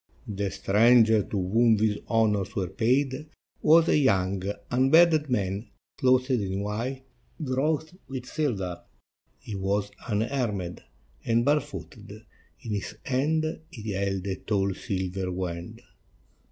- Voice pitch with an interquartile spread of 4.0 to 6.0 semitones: Yes, average, 5.1 semitones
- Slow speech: Yes, slow, 120 wpm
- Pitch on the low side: Yes, low, 110 Hz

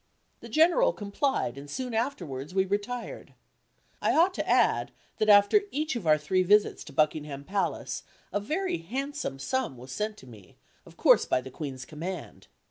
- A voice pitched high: Yes, high, 200 Hz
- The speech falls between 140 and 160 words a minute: No, average, 170 wpm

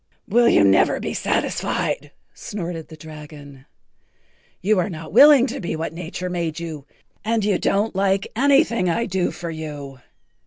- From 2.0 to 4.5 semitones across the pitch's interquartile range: No, average, 5.1 semitones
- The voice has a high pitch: No, medium, 175 Hz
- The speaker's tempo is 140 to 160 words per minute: Yes, average, 155 wpm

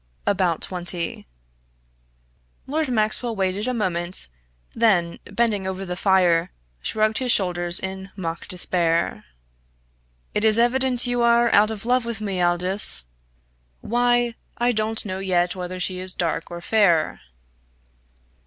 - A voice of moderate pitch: No, high, 195 Hz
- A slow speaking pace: Yes, slow, 130 wpm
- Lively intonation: No, average, 4.5 semitones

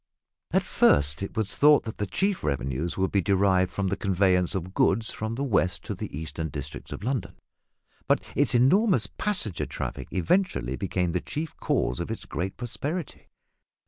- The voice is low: Yes, very low, 95 Hz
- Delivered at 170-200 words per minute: Yes, average, 175 wpm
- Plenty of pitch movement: Yes, wide, 6.4 semitones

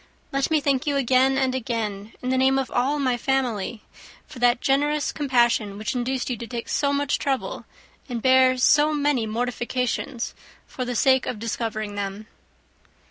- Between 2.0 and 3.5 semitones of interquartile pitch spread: Yes, narrow, 2.5 semitones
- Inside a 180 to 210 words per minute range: No, average, 170 wpm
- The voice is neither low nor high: No, very high, 255 Hz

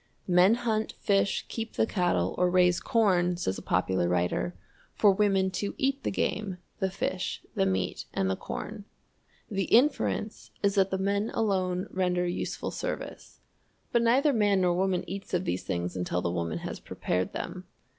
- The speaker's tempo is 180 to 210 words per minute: No, average, 170 wpm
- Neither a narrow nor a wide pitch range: Yes, average, 3.0 semitones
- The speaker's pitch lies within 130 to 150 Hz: No, high, 190 Hz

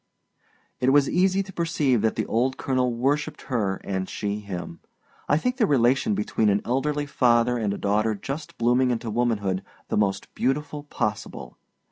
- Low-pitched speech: Yes, low, 125 Hz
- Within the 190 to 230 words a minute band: No, average, 165 wpm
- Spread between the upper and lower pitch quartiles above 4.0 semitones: Yes, wide, 5.5 semitones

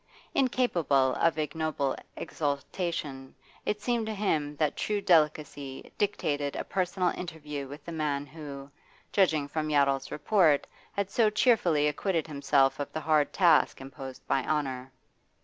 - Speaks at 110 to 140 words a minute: Yes, slow, 135 wpm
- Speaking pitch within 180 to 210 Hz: No, medium, 150 Hz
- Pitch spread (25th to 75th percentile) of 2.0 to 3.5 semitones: No, average, 4.1 semitones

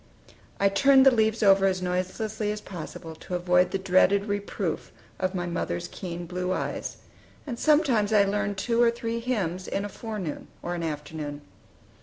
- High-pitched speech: Yes, high, 195 Hz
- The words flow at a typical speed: Yes, average, 170 wpm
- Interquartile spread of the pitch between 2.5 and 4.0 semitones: Yes, average, 3.5 semitones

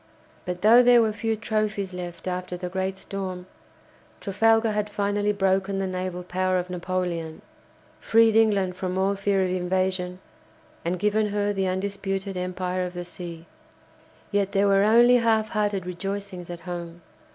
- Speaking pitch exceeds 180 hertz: Yes, high, 190 Hz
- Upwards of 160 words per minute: No, average, 155 wpm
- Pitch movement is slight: Yes, narrow, 2.3 semitones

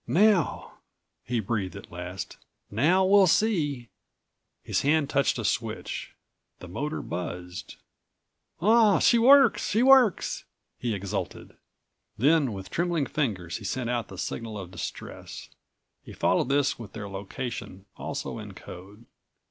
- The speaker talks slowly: Yes, slow, 130 wpm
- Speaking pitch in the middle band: No, low, 125 Hz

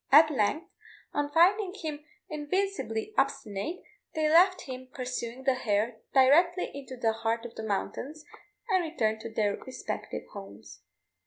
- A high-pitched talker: Yes, very high, 270 Hz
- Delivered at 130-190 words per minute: Yes, average, 140 wpm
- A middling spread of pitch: No, wide, 6.3 semitones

